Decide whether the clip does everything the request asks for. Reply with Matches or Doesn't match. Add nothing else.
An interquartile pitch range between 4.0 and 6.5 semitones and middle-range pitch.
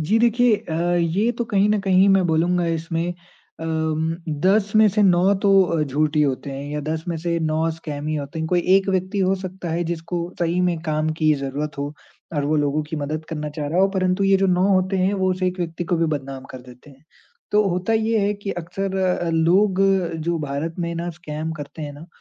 Doesn't match